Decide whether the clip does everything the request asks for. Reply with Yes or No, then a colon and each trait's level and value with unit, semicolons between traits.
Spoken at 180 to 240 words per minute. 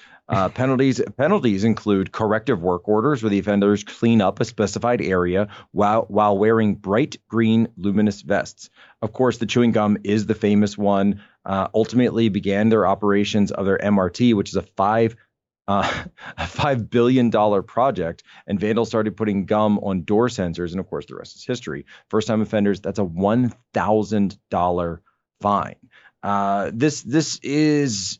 No: average, 160 wpm